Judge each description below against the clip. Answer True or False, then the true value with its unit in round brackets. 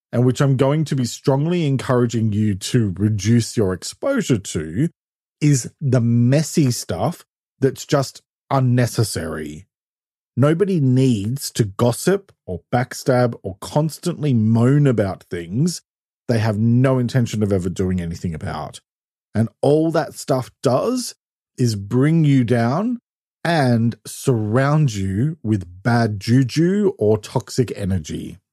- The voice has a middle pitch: False (125 Hz)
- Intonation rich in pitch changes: False (4.7 semitones)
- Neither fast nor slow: False (125 wpm)